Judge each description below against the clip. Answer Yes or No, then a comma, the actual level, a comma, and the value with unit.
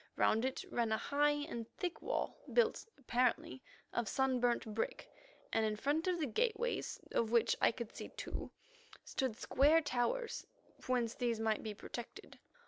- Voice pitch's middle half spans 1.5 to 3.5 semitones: No, average, 4.5 semitones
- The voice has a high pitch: Yes, high, 245 Hz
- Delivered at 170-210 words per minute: No, average, 160 wpm